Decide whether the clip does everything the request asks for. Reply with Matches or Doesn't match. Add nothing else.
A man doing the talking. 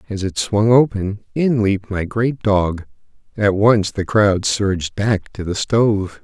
Matches